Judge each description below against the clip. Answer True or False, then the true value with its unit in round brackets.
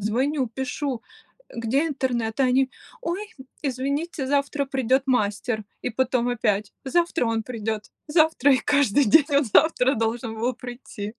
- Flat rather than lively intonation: False (3.8 semitones)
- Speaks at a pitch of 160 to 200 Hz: False (255 Hz)